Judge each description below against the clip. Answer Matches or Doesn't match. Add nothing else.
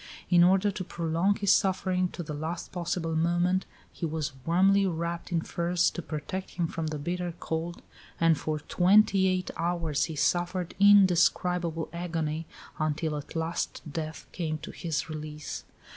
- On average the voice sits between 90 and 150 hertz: Doesn't match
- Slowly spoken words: Doesn't match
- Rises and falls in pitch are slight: Matches